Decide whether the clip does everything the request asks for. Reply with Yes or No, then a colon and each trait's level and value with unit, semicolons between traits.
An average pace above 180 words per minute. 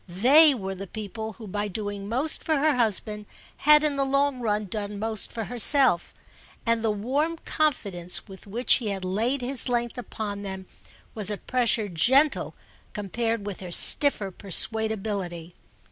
No: average, 160 wpm